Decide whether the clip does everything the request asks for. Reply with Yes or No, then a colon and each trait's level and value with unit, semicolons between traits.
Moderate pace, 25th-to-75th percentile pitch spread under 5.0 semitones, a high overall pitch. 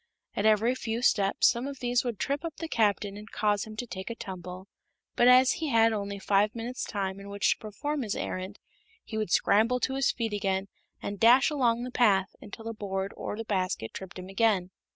No: fast, 215 wpm; average, 3.5 semitones; high, 215 Hz